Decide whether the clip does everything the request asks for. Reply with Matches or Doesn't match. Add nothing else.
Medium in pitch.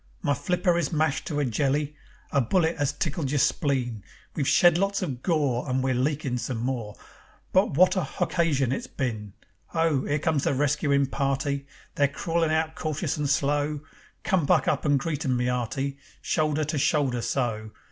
Matches